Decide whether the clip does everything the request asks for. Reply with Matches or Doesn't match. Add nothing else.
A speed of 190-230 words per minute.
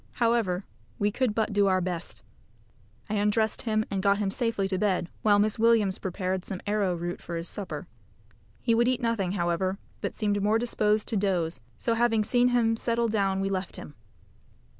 Doesn't match